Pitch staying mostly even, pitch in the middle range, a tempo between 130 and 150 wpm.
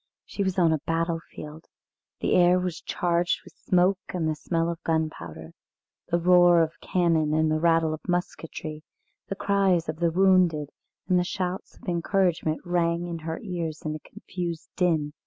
No: narrow, 2.1 semitones; medium, 170 Hz; average, 165 wpm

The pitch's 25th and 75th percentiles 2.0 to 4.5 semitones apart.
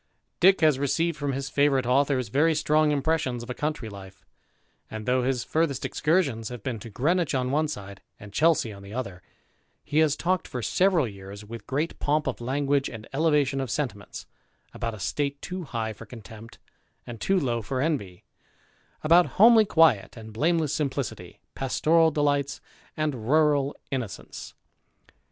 No: average, 4.9 semitones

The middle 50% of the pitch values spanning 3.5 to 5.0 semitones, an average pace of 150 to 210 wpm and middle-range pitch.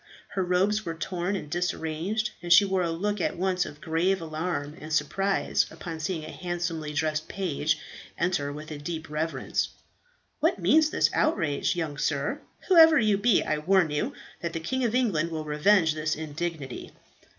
Yes: average, 3.8 semitones; average, 175 wpm; medium, 170 Hz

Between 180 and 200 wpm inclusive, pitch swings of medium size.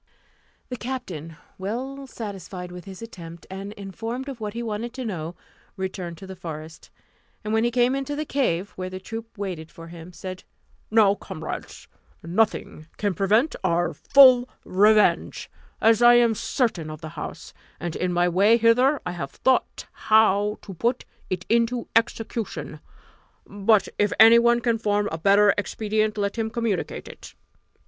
No: average, 160 wpm; average, 4.1 semitones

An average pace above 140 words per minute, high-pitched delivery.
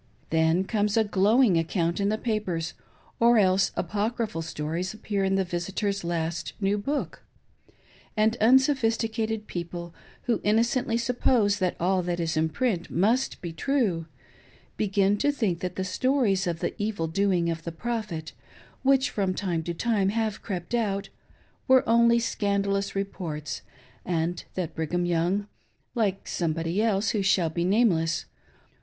Yes: average, 150 wpm; high, 195 Hz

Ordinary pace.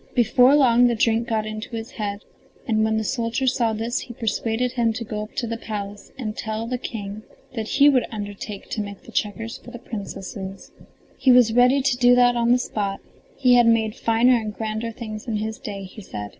No: fast, 215 wpm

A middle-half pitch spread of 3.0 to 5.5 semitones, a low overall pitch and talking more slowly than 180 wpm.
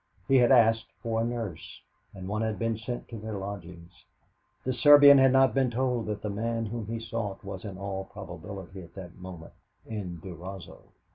No: average, 3.5 semitones; low, 105 Hz; average, 190 wpm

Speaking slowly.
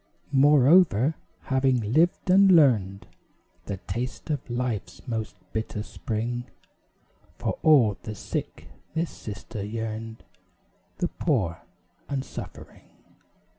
Yes: slow, 100 wpm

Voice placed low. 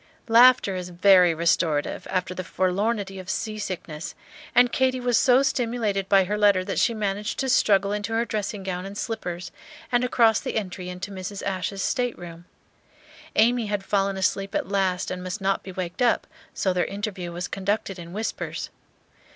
No: high, 195 Hz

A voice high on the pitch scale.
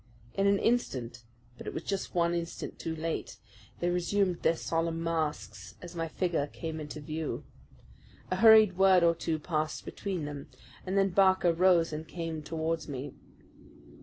No: medium, 165 Hz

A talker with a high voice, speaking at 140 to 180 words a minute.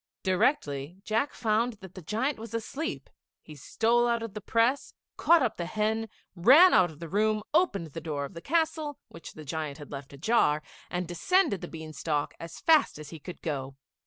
No: high, 195 Hz; average, 195 wpm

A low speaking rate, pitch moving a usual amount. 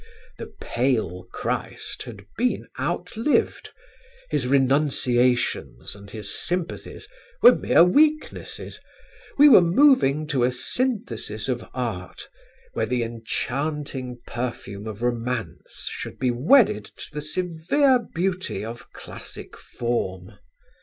No: slow, 110 wpm; wide, 7.2 semitones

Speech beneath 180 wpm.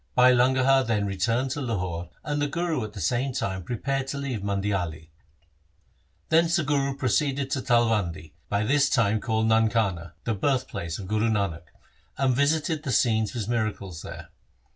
Yes: average, 170 wpm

